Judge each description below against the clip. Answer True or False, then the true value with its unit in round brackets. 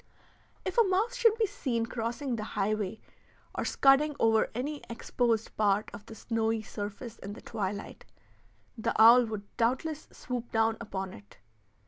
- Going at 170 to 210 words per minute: False (150 wpm)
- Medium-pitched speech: False (230 Hz)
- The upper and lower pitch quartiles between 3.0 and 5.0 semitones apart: True (3.7 semitones)